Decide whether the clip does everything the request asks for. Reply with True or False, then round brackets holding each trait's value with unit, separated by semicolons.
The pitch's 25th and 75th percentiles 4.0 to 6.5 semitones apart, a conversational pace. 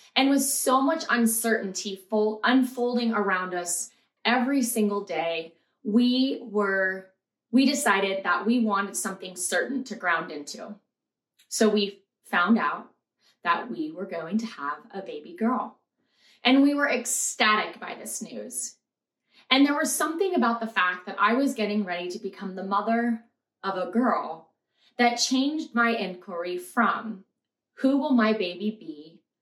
True (4.4 semitones; 150 wpm)